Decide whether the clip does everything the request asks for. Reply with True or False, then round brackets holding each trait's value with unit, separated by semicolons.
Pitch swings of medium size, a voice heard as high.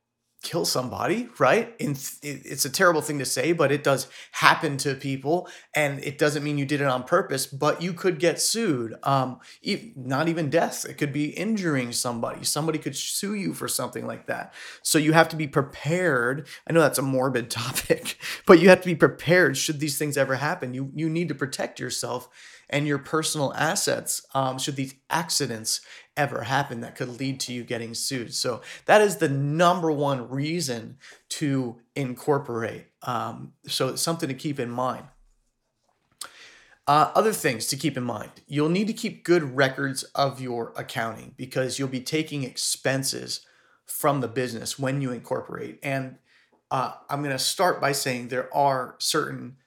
False (3.6 semitones; 140 Hz)